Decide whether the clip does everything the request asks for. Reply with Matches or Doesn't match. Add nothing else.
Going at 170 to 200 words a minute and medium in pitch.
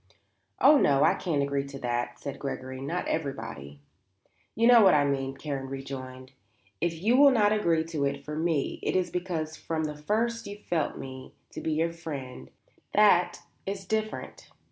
Matches